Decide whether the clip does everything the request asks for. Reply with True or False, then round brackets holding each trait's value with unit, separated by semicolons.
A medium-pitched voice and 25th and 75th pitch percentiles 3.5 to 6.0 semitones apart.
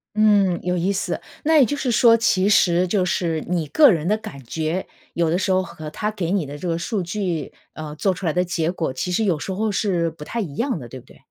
True (180 Hz; 4.1 semitones)